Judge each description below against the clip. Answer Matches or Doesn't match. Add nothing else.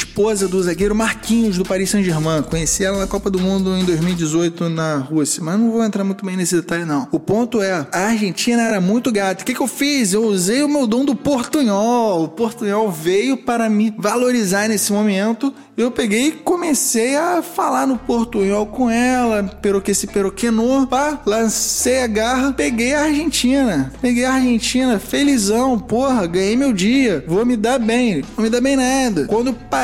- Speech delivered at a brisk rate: Matches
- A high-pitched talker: Matches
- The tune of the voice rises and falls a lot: Doesn't match